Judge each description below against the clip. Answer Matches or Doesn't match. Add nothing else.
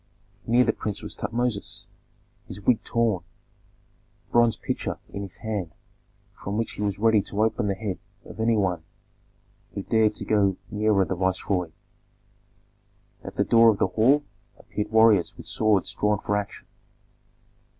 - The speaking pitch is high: Doesn't match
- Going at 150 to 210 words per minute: Matches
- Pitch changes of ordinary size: Doesn't match